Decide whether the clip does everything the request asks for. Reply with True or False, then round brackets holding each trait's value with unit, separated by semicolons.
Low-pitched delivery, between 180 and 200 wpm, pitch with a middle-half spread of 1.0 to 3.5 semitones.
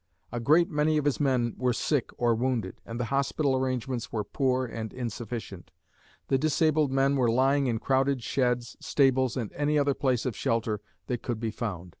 True (130 Hz; 185 wpm; 2.9 semitones)